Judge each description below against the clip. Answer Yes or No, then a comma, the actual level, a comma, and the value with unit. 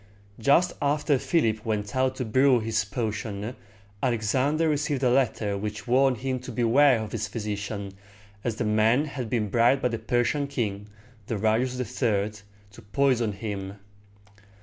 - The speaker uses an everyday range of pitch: Yes, average, 3.6 semitones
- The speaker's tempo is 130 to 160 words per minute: Yes, average, 150 wpm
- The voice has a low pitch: Yes, low, 115 Hz